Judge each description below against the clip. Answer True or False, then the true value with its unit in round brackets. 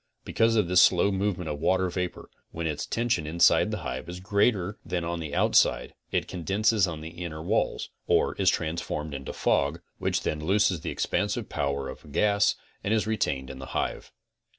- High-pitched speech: False (90 Hz)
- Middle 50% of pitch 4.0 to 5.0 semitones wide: True (4.6 semitones)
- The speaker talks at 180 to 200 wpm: True (190 wpm)